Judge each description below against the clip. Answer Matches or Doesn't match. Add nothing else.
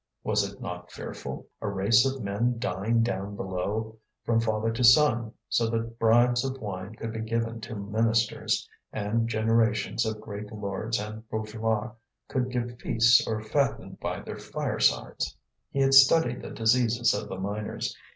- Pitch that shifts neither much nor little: Doesn't match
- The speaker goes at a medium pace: Matches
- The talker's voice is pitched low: Matches